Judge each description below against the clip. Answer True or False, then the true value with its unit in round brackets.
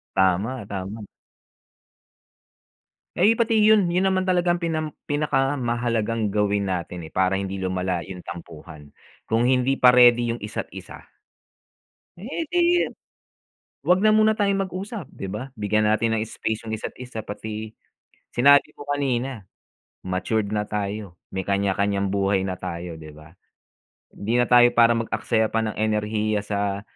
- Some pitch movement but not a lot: False (5.7 semitones)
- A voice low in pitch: True (110 Hz)